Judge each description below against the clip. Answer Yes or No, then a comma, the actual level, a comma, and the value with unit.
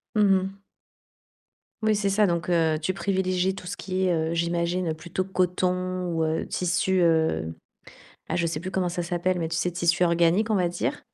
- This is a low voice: No, medium, 180 Hz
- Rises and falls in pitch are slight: Yes, narrow, 1.8 semitones